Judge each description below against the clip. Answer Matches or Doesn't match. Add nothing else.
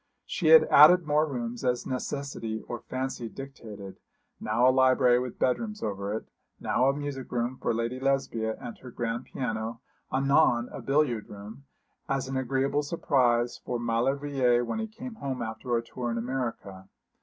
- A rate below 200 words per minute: Matches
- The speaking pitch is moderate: Doesn't match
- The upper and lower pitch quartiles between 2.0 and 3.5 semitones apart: Matches